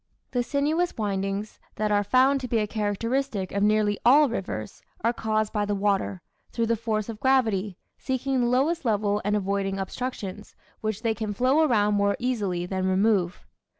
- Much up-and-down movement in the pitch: No, average, 3.6 semitones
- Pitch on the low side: No, high, 215 Hz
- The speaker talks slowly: No, average, 175 wpm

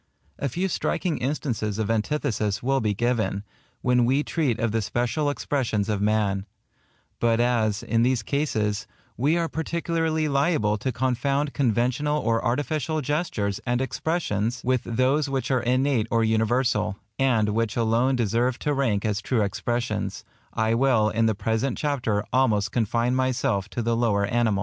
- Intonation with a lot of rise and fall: No, average, 3.9 semitones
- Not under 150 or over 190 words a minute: Yes, average, 155 wpm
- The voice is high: No, low, 120 Hz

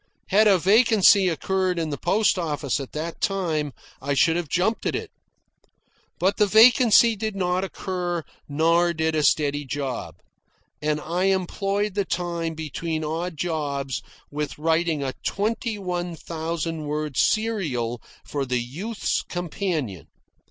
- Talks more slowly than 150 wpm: Yes, average, 140 wpm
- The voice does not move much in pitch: No, average, 4.3 semitones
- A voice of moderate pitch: Yes, medium, 170 Hz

